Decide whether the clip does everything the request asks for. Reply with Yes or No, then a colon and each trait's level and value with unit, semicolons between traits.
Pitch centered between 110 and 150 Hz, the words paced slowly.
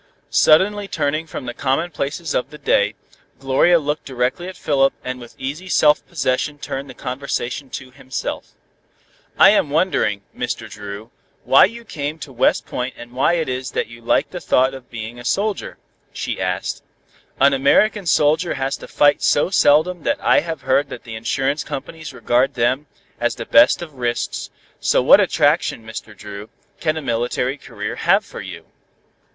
No: low, 135 Hz; average, 170 wpm